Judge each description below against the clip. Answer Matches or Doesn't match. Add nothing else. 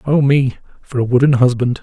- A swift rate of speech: Doesn't match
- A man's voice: Matches